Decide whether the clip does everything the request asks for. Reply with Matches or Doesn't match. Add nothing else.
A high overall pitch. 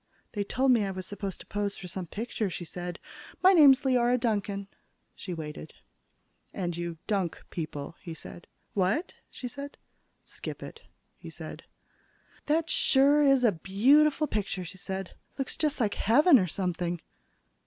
Matches